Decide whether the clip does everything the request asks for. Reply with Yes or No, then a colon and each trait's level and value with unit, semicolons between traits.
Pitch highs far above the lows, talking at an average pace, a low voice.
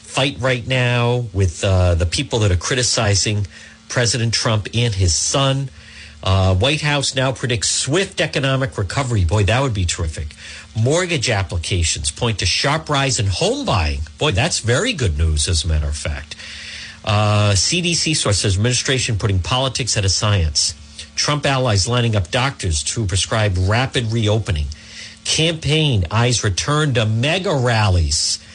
Yes: wide, 6.4 semitones; average, 150 wpm; low, 110 Hz